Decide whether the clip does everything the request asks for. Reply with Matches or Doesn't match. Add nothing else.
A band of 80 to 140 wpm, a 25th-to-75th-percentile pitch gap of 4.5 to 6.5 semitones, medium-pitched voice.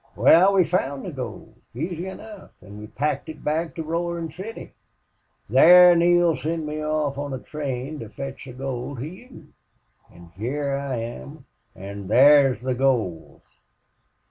Doesn't match